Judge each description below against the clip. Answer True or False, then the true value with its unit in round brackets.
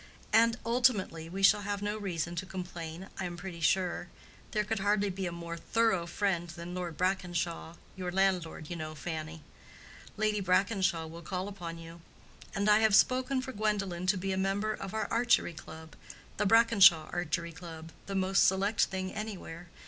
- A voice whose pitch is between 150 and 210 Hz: True (185 Hz)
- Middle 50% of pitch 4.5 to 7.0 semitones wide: False (3.2 semitones)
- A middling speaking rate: True (165 wpm)